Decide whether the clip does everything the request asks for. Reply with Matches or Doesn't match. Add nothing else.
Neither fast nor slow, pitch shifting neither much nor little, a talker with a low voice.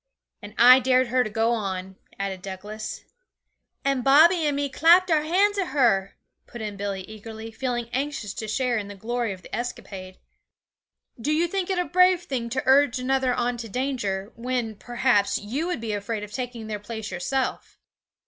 Doesn't match